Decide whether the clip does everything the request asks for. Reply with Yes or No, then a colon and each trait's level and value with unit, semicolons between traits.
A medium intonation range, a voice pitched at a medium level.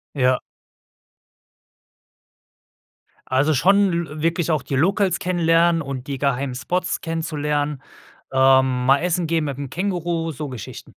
Yes: average, 4.0 semitones; medium, 155 Hz